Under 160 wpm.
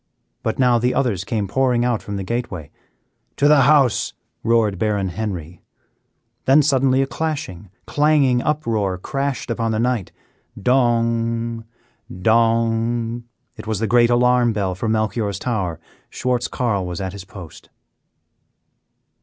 Yes: slow, 135 wpm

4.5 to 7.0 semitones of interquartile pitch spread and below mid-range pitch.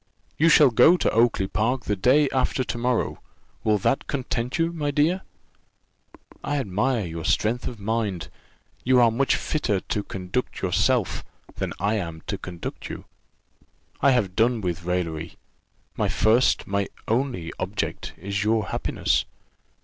Yes: average, 5.1 semitones; low, 110 Hz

